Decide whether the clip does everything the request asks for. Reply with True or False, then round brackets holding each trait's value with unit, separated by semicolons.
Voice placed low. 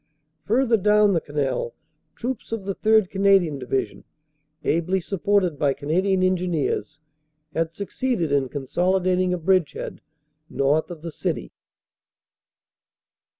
False (180 Hz)